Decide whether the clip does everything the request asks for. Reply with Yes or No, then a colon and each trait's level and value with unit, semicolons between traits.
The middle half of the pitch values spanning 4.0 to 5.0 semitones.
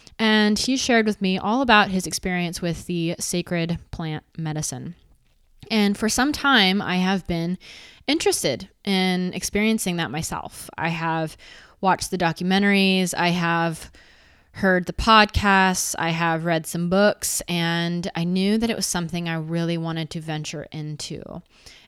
No: average, 3.2 semitones